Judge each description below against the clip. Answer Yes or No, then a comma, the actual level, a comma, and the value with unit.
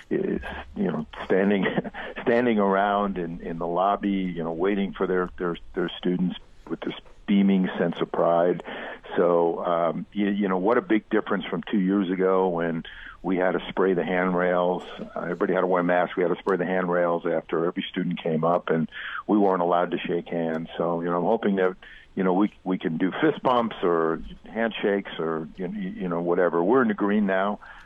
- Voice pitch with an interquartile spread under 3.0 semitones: Yes, narrow, 2.5 semitones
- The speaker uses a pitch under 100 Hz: Yes, very low, 90 Hz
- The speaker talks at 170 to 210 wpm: Yes, average, 200 wpm